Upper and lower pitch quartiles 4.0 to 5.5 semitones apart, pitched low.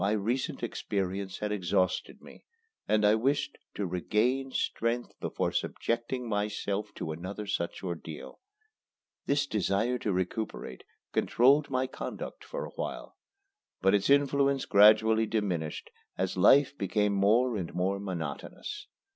Yes: average, 4.6 semitones; low, 105 Hz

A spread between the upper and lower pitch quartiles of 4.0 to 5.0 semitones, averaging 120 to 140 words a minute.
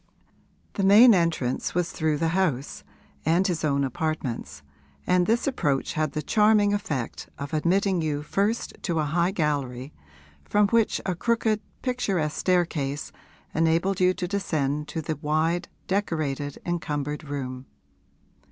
Yes: average, 4.6 semitones; slow, 135 wpm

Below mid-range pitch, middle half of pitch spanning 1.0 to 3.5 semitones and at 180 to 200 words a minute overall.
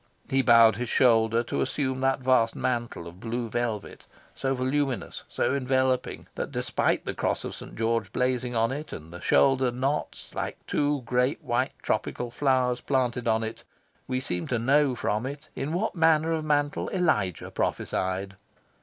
No: low, 125 Hz; average, 2.9 semitones; average, 165 wpm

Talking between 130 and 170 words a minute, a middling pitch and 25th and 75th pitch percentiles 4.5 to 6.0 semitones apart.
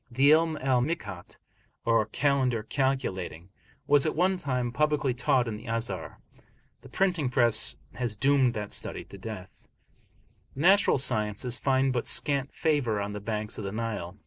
No: average, 160 wpm; low, 125 Hz; average, 4.8 semitones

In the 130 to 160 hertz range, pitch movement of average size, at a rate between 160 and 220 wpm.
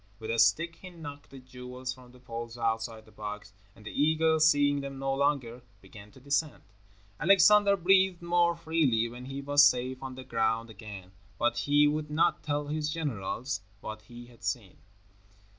Yes: low, 135 Hz; average, 4.9 semitones; average, 175 wpm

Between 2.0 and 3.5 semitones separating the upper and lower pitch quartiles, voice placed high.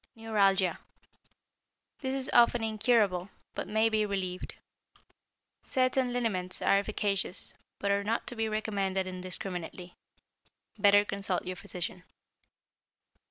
Yes: average, 3.1 semitones; high, 200 Hz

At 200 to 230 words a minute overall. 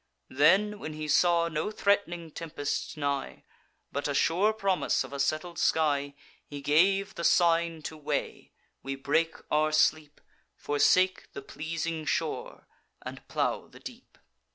No: average, 140 wpm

